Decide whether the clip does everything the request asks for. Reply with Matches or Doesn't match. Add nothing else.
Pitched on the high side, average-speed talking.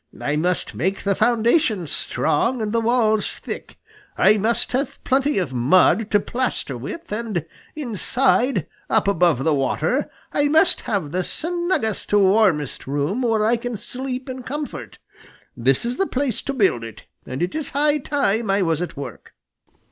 Matches